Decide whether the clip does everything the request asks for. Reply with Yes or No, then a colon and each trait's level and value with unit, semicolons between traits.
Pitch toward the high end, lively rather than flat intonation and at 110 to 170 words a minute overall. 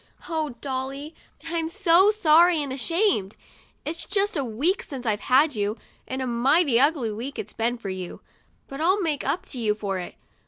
No: very high, 275 Hz; wide, 6.0 semitones; average, 185 wpm